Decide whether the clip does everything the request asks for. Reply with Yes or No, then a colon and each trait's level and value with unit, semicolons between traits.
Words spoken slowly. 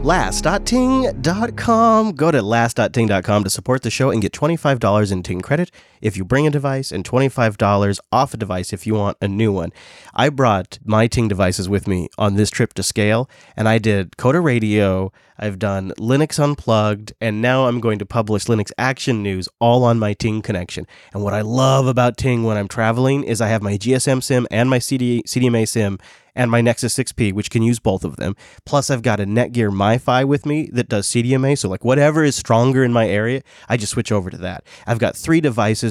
No: fast, 205 wpm